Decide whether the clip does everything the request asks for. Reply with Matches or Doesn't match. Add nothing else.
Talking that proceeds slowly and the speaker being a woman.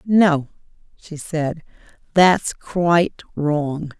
Matches